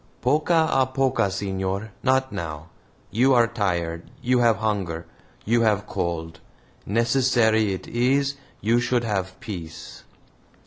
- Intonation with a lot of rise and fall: No, average, 4.9 semitones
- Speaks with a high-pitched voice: No, low, 110 Hz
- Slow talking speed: Yes, slow, 125 wpm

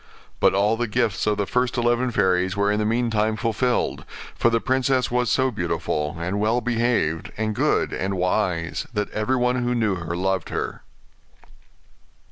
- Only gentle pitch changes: No, average, 4.2 semitones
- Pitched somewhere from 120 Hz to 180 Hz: No, low, 110 Hz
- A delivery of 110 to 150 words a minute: No, average, 165 wpm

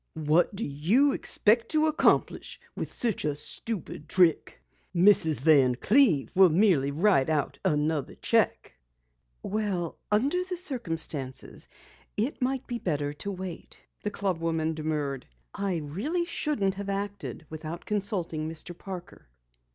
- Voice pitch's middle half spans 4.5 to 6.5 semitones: Yes, wide, 5.5 semitones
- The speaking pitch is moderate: Yes, medium, 180 Hz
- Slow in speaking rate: Yes, slow, 130 wpm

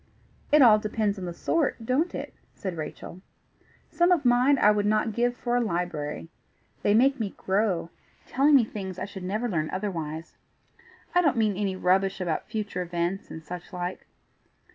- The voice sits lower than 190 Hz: No, high, 205 Hz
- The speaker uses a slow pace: No, average, 175 wpm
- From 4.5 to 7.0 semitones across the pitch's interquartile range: Yes, average, 5.1 semitones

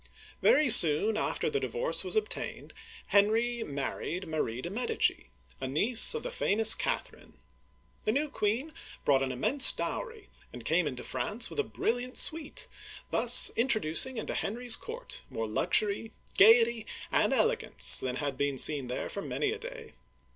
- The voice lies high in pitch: Yes, high, 220 Hz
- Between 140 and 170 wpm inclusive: Yes, average, 155 wpm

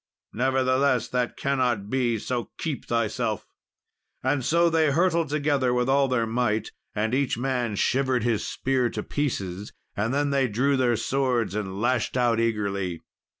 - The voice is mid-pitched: No, low, 125 Hz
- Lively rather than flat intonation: No, average, 3.2 semitones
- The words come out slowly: No, average, 150 wpm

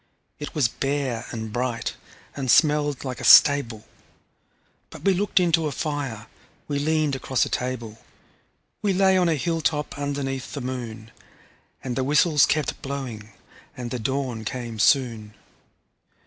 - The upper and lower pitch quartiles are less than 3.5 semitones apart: No, average, 3.8 semitones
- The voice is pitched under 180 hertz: Yes, low, 135 Hz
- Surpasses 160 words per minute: No, average, 145 wpm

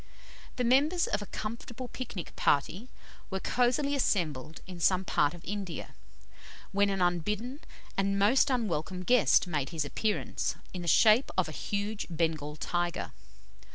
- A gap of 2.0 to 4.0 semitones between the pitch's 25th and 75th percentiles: No, wide, 5.6 semitones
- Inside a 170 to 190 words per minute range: No, average, 150 wpm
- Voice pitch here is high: Yes, high, 195 Hz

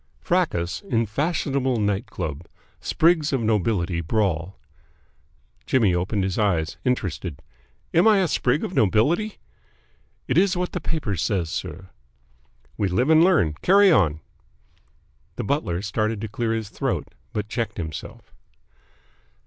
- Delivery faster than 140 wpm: No, slow, 135 wpm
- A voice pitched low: Yes, low, 110 Hz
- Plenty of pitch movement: Yes, wide, 7.8 semitones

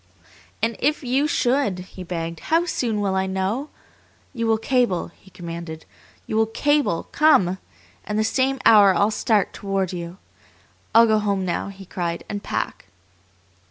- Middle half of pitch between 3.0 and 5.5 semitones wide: Yes, average, 4.6 semitones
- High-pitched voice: Yes, high, 205 Hz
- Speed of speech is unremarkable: Yes, average, 160 wpm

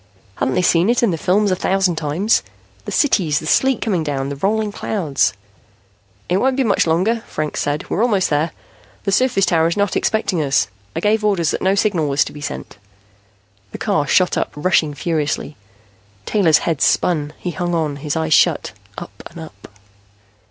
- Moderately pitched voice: Yes, medium, 170 Hz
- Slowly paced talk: No, average, 185 wpm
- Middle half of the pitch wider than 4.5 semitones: Yes, average, 5.1 semitones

